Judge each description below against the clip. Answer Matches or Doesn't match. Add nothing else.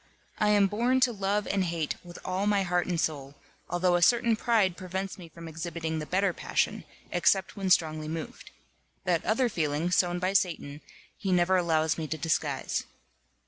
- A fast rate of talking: Doesn't match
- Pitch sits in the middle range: Matches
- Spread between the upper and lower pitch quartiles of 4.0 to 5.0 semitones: Doesn't match